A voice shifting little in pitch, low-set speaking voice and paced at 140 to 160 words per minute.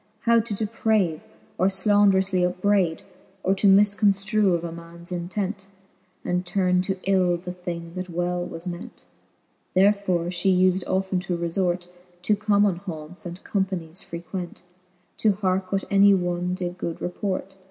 No: narrow, 2.0 semitones; medium, 185 Hz; average, 145 wpm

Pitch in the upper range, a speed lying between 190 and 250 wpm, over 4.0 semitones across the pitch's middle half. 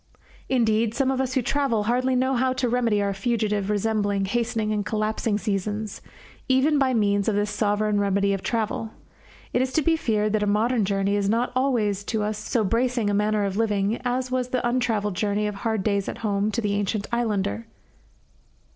No: high, 215 Hz; average, 195 wpm; average, 3.1 semitones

